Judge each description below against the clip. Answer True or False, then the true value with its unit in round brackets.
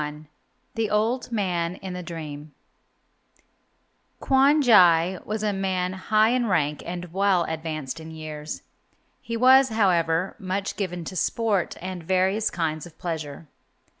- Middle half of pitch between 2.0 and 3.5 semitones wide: False (4.5 semitones)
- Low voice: False (180 Hz)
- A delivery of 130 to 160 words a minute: True (135 wpm)